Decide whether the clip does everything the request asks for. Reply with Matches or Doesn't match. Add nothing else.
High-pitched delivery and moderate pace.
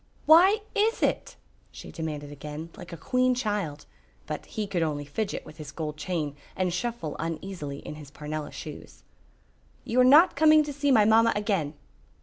Doesn't match